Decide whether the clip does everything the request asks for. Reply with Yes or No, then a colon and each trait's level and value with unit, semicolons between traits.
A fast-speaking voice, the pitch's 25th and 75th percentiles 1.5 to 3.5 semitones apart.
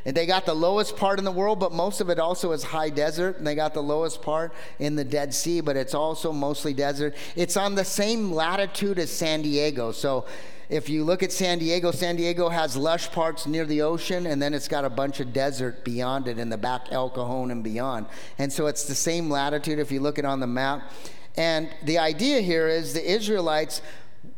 Yes: fast, 225 wpm; average, 3.2 semitones